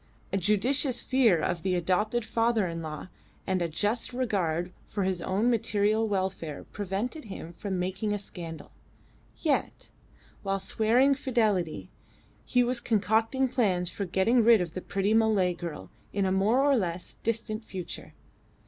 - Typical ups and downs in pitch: Yes, average, 4.1 semitones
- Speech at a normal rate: Yes, average, 150 wpm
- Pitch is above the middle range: Yes, high, 205 Hz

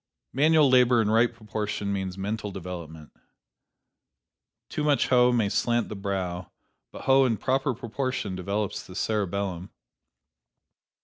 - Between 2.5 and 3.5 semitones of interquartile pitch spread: No, average, 4.4 semitones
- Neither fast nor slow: No, slow, 125 wpm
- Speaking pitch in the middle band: No, low, 105 Hz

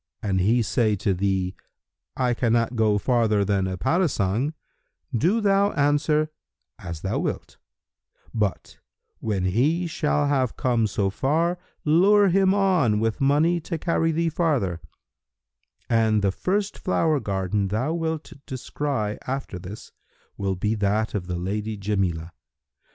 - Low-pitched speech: Yes, low, 115 Hz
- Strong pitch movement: Yes, wide, 7.9 semitones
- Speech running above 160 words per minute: No, slow, 135 wpm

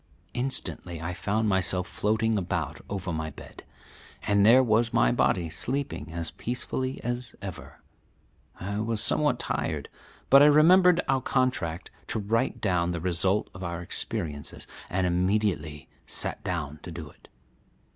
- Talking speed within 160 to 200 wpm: No, average, 145 wpm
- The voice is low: Yes, low, 100 Hz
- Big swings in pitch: Yes, wide, 5.7 semitones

